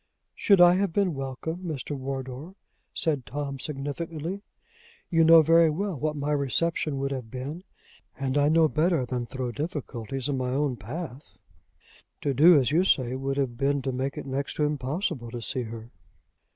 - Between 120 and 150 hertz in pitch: Yes, medium, 140 Hz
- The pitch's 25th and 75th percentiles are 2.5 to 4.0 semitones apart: Yes, average, 3.6 semitones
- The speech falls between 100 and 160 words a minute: No, average, 175 wpm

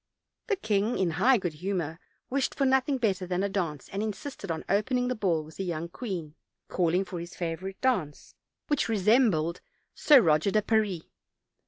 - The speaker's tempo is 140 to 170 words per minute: No, average, 180 wpm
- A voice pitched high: Yes, high, 195 Hz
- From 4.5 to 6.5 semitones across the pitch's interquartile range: Yes, average, 5.2 semitones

